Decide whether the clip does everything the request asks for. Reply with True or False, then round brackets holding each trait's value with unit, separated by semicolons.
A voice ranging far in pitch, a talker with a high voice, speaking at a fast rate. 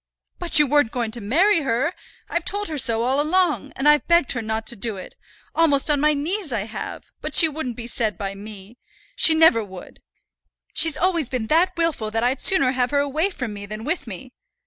True (6.2 semitones; 270 Hz; 215 wpm)